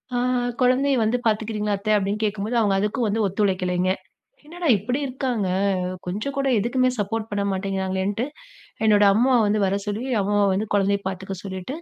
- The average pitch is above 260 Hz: No, high, 210 Hz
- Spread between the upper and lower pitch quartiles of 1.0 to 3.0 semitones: No, average, 3.6 semitones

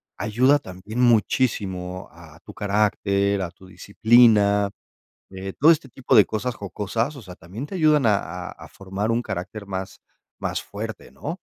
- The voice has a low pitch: Yes, low, 105 Hz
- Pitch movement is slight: No, average, 4.1 semitones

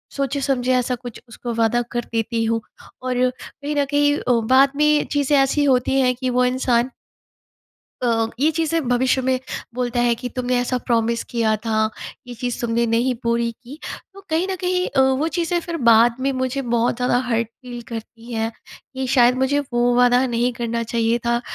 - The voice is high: Yes, very high, 250 Hz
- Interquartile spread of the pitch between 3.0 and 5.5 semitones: No, narrow, 2.5 semitones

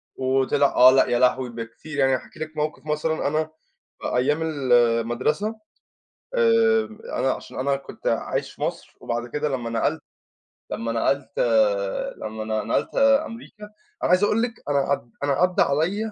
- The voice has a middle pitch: Yes, medium, 145 Hz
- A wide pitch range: Yes, wide, 6.7 semitones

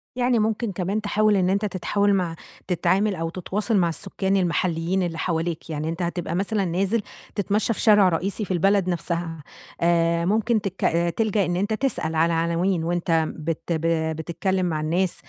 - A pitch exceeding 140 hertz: Yes, medium, 185 Hz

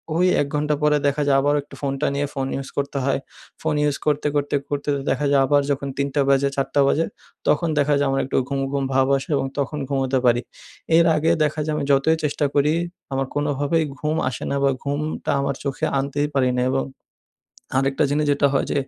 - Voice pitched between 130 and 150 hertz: Yes, medium, 140 Hz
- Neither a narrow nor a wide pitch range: No, narrow, 1.4 semitones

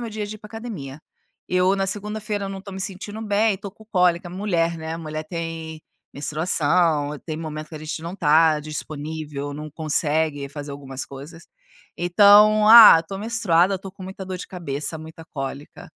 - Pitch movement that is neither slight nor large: Yes, average, 4.4 semitones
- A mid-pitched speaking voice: Yes, medium, 170 Hz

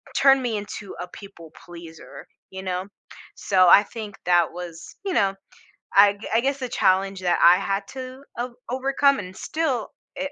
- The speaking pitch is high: Yes, high, 200 Hz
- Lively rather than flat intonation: Yes, wide, 5.7 semitones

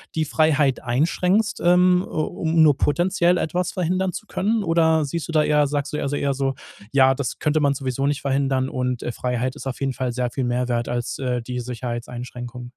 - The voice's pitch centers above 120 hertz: Yes, medium, 140 Hz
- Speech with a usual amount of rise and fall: Yes, average, 4.3 semitones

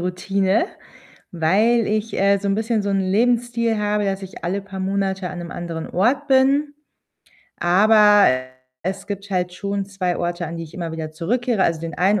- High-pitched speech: Yes, high, 195 Hz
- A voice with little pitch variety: No, average, 3.2 semitones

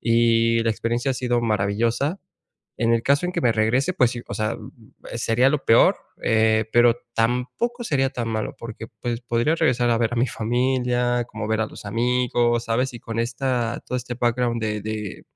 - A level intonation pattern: Yes, narrow, 1.7 semitones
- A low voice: Yes, low, 120 Hz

